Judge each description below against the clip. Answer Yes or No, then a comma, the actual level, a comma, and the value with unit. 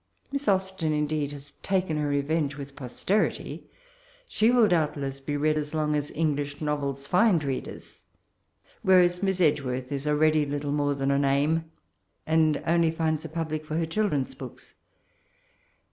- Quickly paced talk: No, average, 160 wpm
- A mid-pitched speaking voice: Yes, medium, 150 Hz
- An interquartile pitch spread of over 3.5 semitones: No, narrow, 2.4 semitones